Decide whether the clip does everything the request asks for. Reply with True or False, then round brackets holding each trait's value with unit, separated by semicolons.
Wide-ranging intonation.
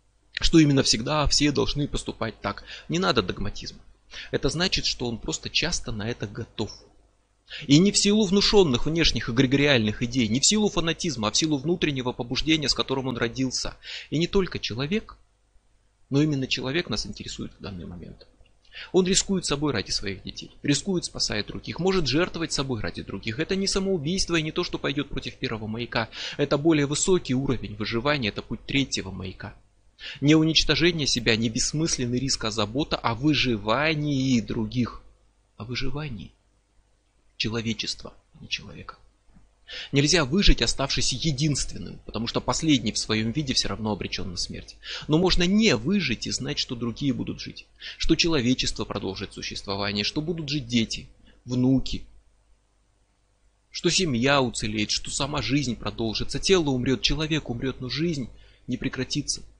True (6.2 semitones)